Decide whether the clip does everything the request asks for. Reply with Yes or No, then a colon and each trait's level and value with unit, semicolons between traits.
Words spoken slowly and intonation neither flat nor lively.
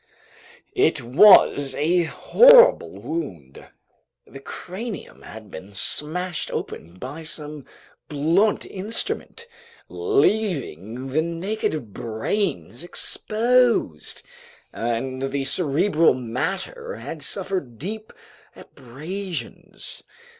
No: slow, 80 wpm; wide, 7.8 semitones